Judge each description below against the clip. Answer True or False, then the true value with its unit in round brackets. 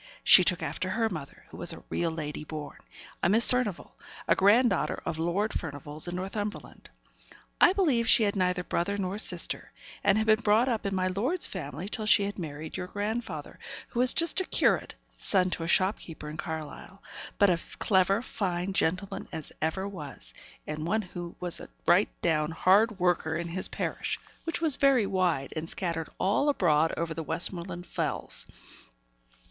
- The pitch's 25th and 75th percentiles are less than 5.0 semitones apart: True (4.3 semitones)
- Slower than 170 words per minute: False (180 wpm)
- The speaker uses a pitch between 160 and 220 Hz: True (185 Hz)